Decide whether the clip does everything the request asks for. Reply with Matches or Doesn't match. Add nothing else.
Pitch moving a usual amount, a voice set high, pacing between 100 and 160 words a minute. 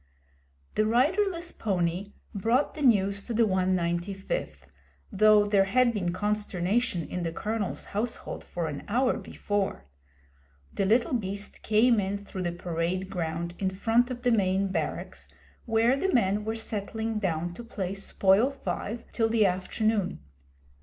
Matches